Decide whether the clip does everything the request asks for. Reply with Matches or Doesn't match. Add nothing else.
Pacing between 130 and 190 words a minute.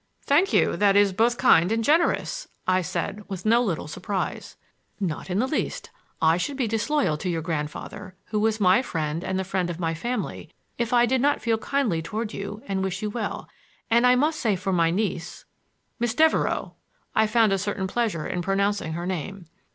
Doesn't match